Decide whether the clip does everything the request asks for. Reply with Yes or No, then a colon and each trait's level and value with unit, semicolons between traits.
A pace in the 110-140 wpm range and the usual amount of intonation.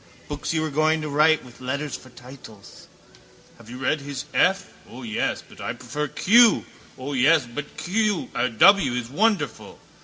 No: average, 155 wpm; average, 4.0 semitones